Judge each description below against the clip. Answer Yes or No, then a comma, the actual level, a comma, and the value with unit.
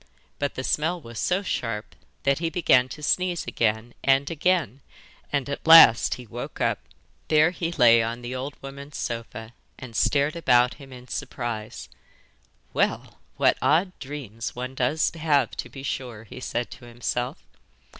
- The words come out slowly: No, average, 160 wpm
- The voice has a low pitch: Yes, low, 130 Hz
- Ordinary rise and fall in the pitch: Yes, average, 4.2 semitones